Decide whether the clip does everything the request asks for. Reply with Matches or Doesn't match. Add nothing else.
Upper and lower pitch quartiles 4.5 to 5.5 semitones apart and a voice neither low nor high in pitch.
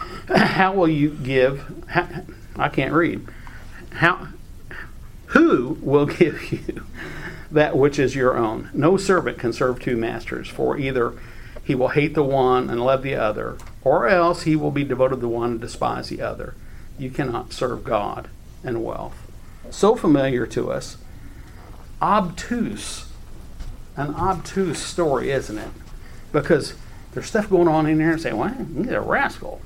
Matches